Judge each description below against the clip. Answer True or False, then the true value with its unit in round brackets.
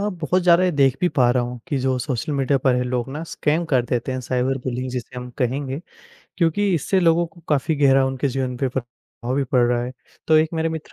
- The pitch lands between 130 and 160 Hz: True (135 Hz)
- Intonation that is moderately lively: True (4.2 semitones)